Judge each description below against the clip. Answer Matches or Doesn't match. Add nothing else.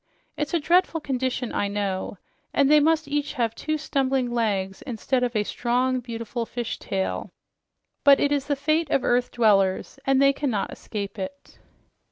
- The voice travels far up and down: Doesn't match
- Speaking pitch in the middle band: Doesn't match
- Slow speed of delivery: Doesn't match